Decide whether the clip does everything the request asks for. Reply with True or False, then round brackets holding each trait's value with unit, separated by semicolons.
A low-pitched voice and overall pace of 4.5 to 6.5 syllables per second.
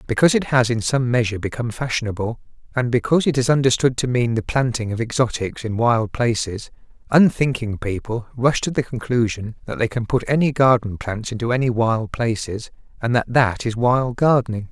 True (120 Hz; 5.5 syllables/s)